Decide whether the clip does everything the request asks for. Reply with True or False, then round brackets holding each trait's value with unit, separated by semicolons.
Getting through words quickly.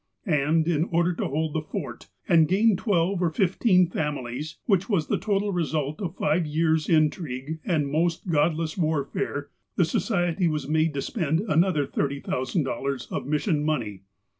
False (155 wpm)